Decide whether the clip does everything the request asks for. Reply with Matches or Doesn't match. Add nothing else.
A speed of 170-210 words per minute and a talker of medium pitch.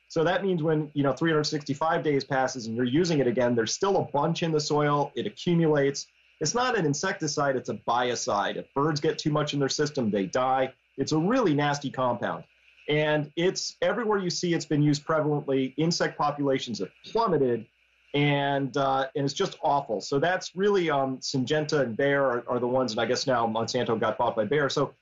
Matches